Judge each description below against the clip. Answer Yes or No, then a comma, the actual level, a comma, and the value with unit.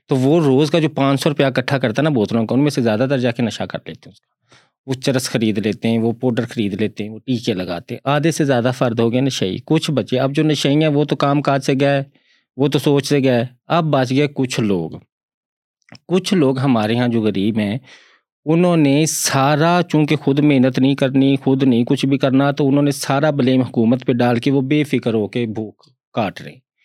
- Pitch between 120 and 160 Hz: Yes, low, 135 Hz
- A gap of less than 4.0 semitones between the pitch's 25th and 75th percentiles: Yes, average, 3.1 semitones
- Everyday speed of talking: No, fast, 240 wpm